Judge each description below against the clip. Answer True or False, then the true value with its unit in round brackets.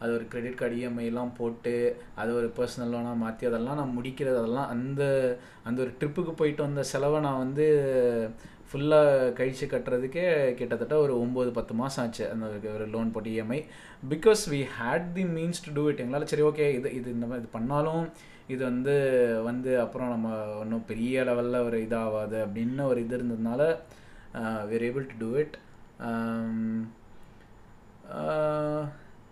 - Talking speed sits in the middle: False (150 wpm)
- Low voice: True (125 Hz)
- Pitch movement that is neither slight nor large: True (3.4 semitones)